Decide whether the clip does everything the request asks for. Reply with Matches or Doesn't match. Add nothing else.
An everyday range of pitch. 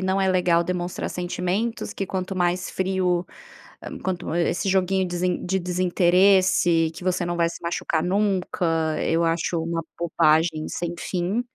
Doesn't match